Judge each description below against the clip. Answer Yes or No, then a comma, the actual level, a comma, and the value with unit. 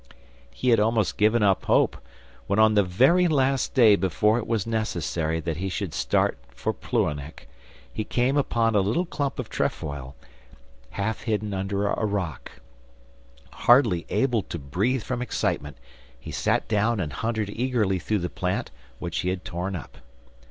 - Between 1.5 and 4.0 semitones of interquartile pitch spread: No, average, 4.5 semitones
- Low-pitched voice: Yes, low, 105 Hz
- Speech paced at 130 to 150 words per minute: No, average, 160 wpm